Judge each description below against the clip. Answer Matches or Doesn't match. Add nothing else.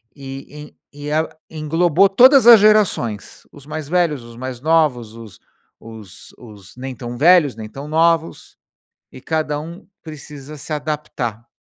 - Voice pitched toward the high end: Doesn't match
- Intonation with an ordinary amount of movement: Matches